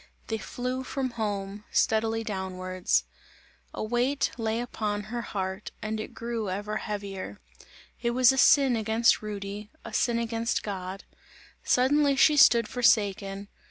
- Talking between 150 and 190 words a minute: No, slow, 135 wpm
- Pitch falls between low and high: No, high, 220 Hz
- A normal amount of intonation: Yes, average, 3.1 semitones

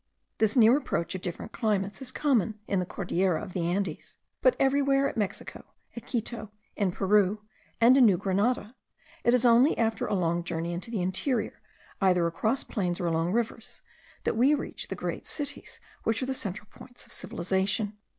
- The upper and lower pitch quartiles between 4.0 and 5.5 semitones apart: Yes, average, 4.8 semitones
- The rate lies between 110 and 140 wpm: No, average, 180 wpm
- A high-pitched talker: Yes, high, 210 Hz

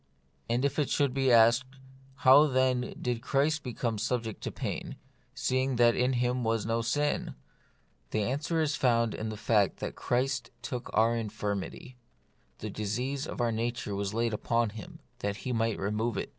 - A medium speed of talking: Yes, average, 170 wpm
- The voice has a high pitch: No, low, 120 Hz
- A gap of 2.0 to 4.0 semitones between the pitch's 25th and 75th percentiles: Yes, narrow, 2.6 semitones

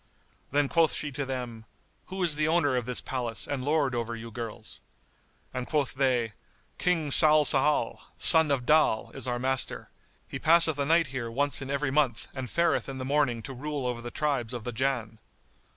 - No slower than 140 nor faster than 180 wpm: No, average, 190 wpm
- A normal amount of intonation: Yes, average, 3.6 semitones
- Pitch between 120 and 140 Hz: Yes, low, 135 Hz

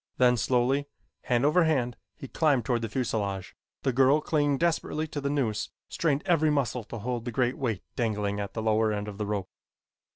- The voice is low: Yes, low, 125 Hz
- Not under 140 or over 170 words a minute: No, average, 195 wpm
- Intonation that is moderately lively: Yes, average, 4.5 semitones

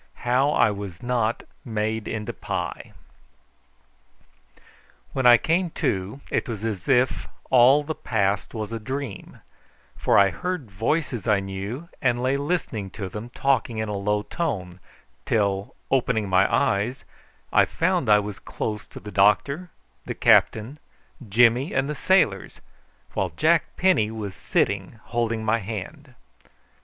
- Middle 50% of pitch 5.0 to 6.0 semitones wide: No, average, 4.6 semitones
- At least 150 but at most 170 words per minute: No, average, 140 wpm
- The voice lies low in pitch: Yes, low, 110 Hz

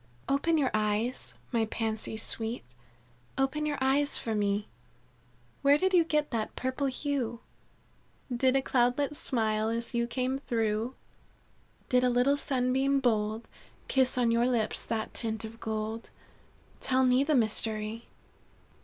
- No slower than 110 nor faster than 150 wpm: Yes, slow, 135 wpm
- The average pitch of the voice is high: Yes, high, 245 Hz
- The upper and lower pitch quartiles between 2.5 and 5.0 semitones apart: Yes, average, 3.4 semitones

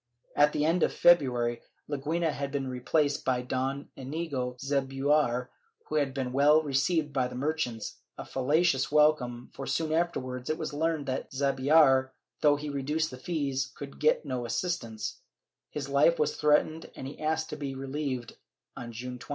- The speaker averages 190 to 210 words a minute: No, average, 170 wpm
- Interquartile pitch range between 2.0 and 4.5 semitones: Yes, average, 2.9 semitones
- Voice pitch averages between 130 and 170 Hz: Yes, medium, 140 Hz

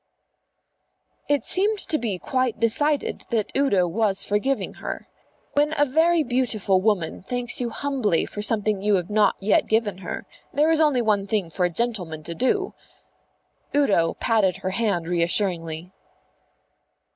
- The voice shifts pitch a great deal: Yes, wide, 5.9 semitones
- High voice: Yes, high, 215 Hz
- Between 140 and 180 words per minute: Yes, average, 145 wpm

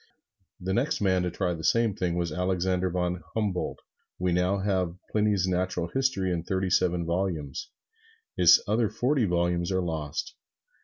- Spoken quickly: No, average, 155 wpm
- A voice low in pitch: Yes, very low, 90 Hz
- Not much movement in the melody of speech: Yes, narrow, 2.1 semitones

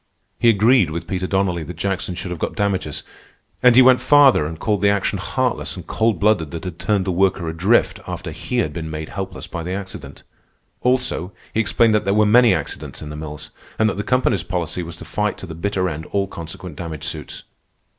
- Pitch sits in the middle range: No, very low, 95 Hz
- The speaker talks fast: Yes, fast, 215 wpm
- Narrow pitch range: No, average, 4.0 semitones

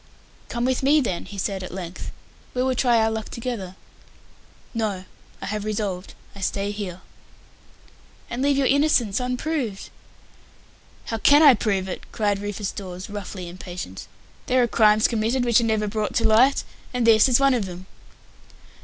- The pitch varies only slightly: No, average, 4.1 semitones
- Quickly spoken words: No, average, 165 wpm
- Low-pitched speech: No, high, 215 Hz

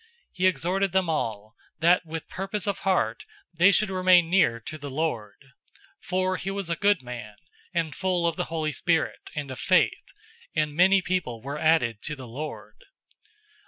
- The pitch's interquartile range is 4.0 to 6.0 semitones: Yes, average, 5.3 semitones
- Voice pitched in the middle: Yes, medium, 165 Hz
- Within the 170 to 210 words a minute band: Yes, average, 175 wpm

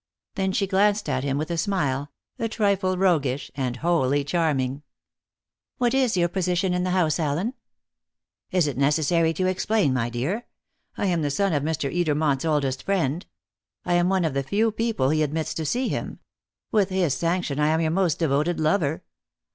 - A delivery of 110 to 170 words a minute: No, average, 180 wpm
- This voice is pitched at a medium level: Yes, medium, 165 Hz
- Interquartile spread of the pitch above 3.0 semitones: Yes, average, 4.7 semitones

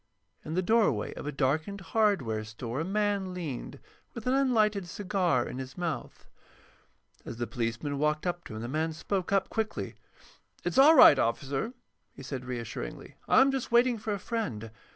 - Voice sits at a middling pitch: Yes, medium, 170 Hz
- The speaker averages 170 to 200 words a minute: Yes, average, 175 wpm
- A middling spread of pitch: No, wide, 8.5 semitones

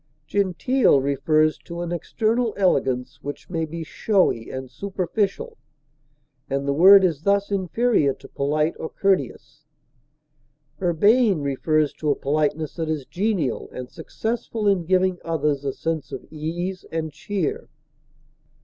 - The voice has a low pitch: No, medium, 165 Hz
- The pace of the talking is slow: Yes, slow, 130 wpm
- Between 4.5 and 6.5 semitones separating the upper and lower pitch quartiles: Yes, average, 4.9 semitones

